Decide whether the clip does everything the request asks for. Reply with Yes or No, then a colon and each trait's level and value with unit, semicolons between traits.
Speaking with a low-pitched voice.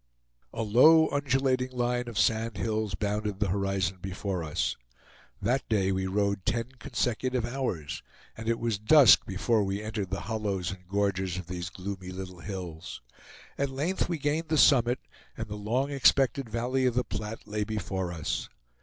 Yes: low, 105 Hz